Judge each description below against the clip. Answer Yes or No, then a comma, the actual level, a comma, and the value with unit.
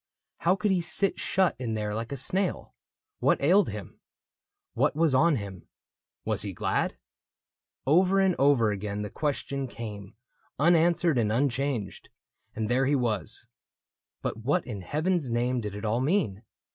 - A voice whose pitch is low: Yes, low, 130 Hz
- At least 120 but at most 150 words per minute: No, average, 160 wpm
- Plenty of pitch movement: Yes, wide, 7.6 semitones